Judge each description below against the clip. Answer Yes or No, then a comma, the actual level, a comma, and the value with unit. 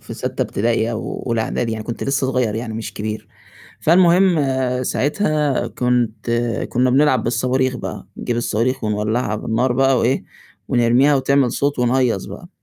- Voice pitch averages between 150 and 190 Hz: No, low, 125 Hz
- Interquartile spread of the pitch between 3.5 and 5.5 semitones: No, average, 2.8 semitones